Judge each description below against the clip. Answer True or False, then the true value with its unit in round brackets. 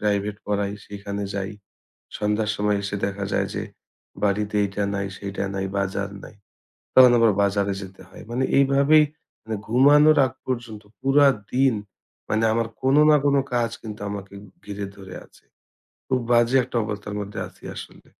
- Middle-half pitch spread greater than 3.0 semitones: True (3.7 semitones)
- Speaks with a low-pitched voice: True (105 Hz)